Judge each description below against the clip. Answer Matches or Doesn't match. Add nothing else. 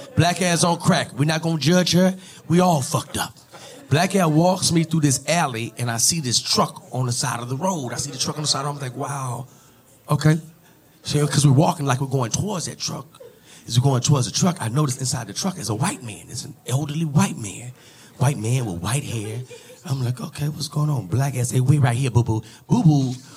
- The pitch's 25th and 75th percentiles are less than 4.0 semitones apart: Doesn't match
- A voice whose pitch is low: Doesn't match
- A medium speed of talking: Doesn't match